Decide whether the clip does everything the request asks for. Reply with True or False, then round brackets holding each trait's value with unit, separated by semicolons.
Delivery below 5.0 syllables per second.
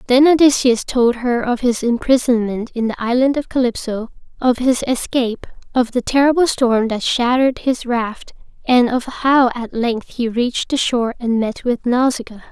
True (4.8 syllables/s)